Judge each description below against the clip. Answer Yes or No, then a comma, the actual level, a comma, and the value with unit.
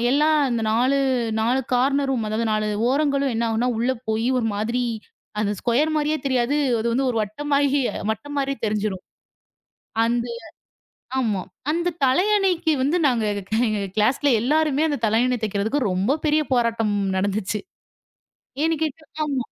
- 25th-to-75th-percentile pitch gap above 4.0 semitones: Yes, average, 4.7 semitones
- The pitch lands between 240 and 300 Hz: Yes, very high, 250 Hz